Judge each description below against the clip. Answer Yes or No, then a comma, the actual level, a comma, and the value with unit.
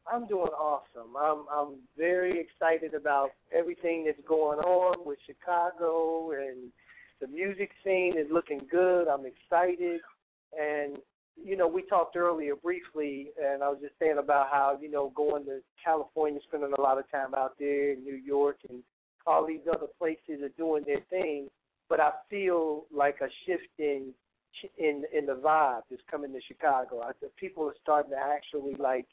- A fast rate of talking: No, average, 170 wpm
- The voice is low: No, medium, 150 Hz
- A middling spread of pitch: Yes, average, 3.3 semitones